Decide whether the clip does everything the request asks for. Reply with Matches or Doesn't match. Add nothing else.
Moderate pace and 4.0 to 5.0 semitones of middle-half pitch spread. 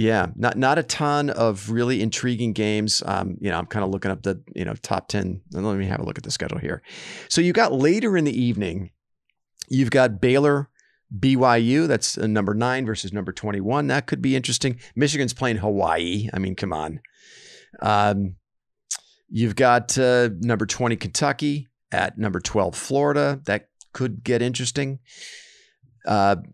Matches